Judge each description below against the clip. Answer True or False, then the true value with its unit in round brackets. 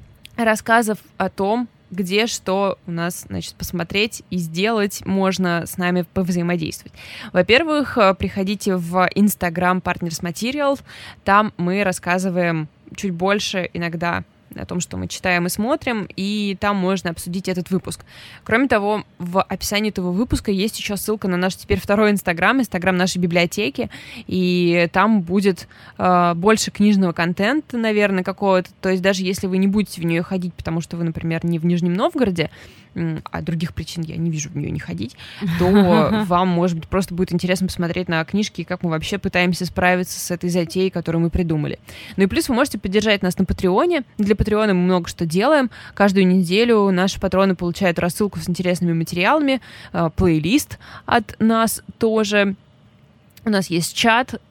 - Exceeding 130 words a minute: True (160 wpm)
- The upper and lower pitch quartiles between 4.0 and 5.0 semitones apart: False (2.8 semitones)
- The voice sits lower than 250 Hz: True (185 Hz)